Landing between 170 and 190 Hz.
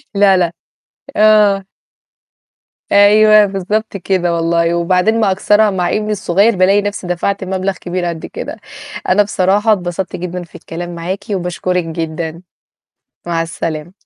Yes: medium, 185 Hz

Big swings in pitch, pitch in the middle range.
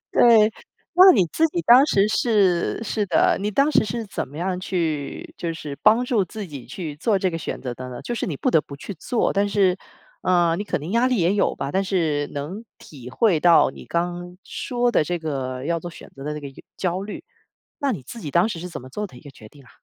Yes: wide, 5.9 semitones; medium, 180 Hz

